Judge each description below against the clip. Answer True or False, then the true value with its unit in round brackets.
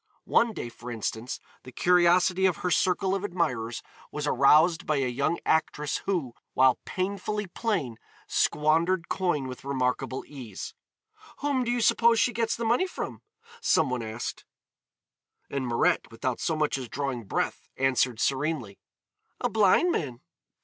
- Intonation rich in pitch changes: True (6.7 semitones)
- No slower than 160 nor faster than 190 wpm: False (150 wpm)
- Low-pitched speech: False (150 Hz)